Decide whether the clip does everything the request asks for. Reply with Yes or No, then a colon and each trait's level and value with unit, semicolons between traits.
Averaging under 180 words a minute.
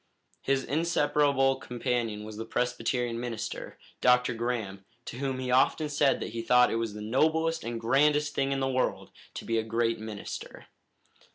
Yes: average, 170 wpm